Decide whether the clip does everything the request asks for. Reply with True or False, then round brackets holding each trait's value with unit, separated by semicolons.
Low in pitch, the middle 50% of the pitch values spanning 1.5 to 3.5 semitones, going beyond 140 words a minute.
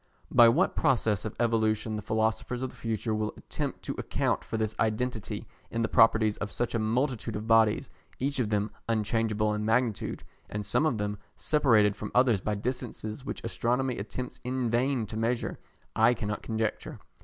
True (110 Hz; 2.4 semitones; 180 wpm)